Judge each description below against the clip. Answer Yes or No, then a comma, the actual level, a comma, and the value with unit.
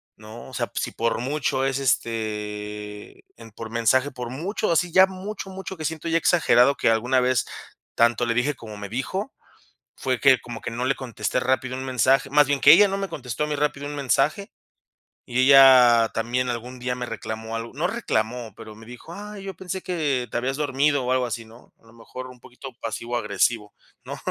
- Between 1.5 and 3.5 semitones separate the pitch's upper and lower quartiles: No, average, 4.1 semitones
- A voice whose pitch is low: Yes, low, 125 Hz